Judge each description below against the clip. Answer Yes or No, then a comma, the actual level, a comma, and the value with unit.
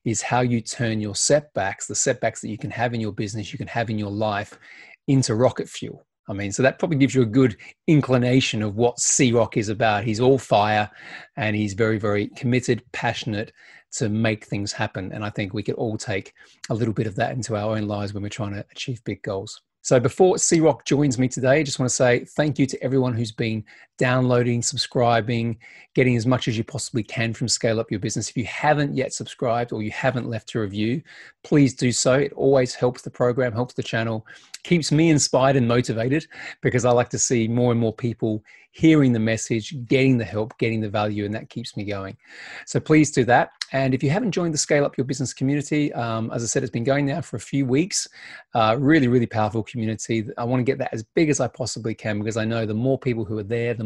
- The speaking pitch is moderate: No, low, 120 Hz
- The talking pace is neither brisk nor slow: No, fast, 235 wpm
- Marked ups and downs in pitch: No, average, 3.3 semitones